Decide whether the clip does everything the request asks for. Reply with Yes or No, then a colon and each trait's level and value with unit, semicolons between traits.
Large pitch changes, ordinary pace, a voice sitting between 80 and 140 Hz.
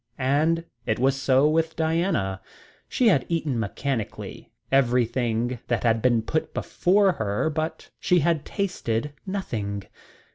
No: wide, 6.0 semitones; slow, 130 wpm; low, 135 Hz